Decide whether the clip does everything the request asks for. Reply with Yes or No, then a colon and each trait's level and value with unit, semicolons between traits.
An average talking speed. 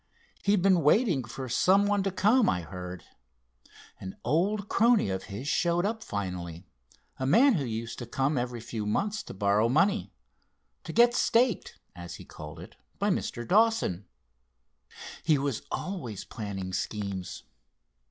Yes: average, 150 wpm